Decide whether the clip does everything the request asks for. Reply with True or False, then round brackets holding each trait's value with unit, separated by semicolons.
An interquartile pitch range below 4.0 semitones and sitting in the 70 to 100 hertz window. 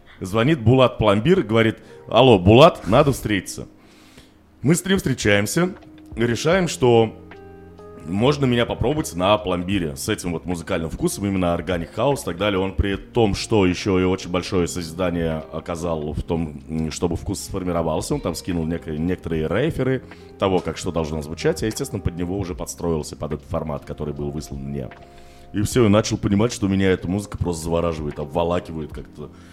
False (4.5 semitones; 90 Hz)